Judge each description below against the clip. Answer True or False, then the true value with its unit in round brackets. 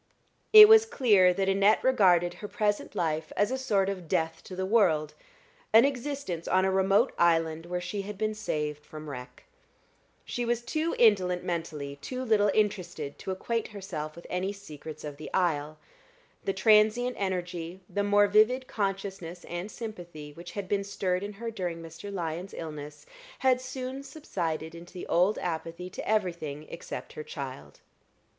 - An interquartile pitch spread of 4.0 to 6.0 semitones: True (4.4 semitones)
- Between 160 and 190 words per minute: True (165 wpm)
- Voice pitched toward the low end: False (190 Hz)